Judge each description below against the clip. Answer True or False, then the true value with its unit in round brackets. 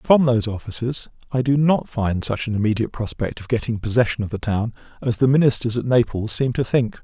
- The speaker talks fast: True (215 wpm)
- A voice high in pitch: False (115 Hz)